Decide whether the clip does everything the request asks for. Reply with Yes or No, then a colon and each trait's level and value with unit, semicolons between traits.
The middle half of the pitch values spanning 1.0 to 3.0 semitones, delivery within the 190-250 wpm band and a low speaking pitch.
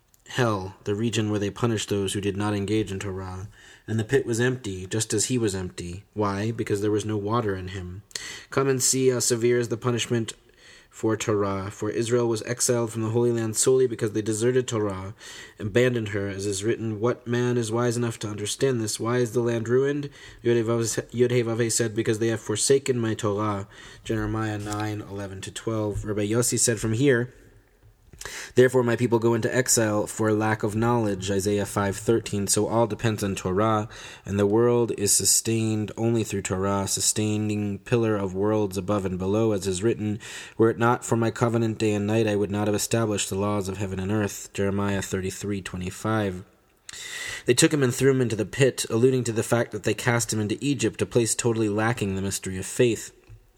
Yes: narrow, 2.6 semitones; average, 195 wpm; low, 110 Hz